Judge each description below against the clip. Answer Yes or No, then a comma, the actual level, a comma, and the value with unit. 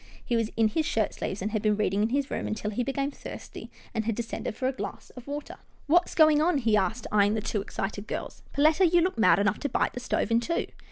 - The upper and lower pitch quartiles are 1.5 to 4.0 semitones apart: No, average, 5.1 semitones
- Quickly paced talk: Yes, fast, 255 wpm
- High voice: Yes, high, 230 Hz